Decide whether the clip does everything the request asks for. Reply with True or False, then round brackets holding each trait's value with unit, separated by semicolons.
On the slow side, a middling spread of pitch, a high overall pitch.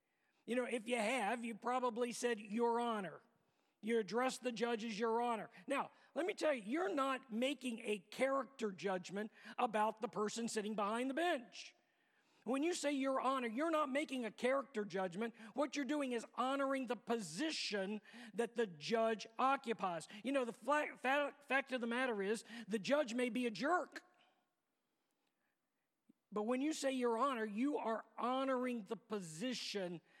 False (165 wpm; 3.4 semitones; 245 Hz)